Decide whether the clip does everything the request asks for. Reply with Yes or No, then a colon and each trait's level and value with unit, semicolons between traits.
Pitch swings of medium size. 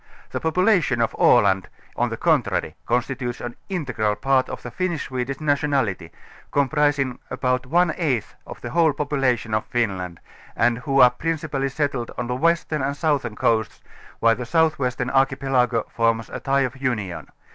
Yes: average, 3.5 semitones